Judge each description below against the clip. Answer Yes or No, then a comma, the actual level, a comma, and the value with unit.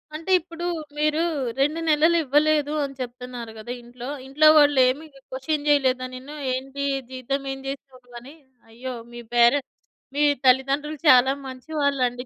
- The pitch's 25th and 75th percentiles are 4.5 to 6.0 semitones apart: No, average, 2.8 semitones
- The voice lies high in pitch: Yes, very high, 275 Hz